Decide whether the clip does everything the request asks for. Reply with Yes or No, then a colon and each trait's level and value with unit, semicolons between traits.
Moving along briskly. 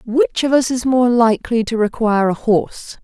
No: average, 195 wpm